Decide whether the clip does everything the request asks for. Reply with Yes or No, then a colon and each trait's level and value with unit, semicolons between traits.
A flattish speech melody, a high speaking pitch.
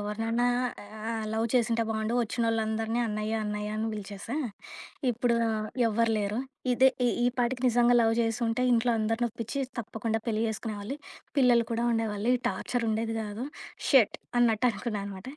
Yes: narrow, 1.8 semitones; high, 225 Hz